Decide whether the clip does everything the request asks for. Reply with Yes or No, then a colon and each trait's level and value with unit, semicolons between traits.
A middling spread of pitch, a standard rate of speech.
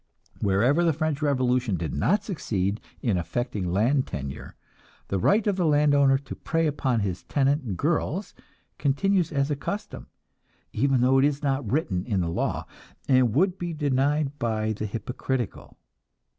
No: wide, 5.7 semitones; average, 155 wpm